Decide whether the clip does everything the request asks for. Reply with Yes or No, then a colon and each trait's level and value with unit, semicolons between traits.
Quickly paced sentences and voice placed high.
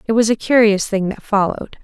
Yes: fast, 230 wpm; high, 210 Hz